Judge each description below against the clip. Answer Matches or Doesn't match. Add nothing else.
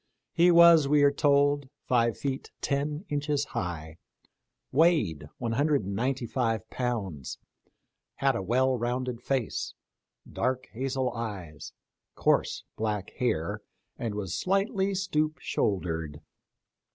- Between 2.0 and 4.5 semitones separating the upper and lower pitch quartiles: Doesn't match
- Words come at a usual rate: Doesn't match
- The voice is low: Matches